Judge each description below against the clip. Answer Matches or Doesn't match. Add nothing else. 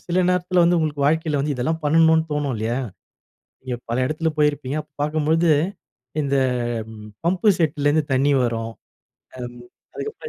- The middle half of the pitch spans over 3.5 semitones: Doesn't match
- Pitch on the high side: Doesn't match